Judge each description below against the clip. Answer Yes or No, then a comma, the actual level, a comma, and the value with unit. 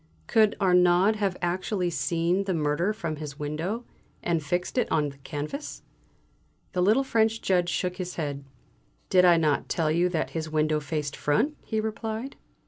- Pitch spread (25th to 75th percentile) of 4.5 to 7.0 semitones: Yes, average, 4.8 semitones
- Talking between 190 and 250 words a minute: No, average, 165 wpm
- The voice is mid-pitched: Yes, medium, 175 Hz